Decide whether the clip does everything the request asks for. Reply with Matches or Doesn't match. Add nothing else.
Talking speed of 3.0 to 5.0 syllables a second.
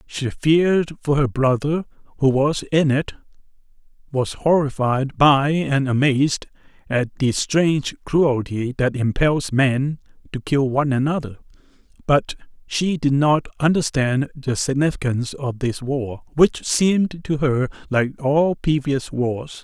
Matches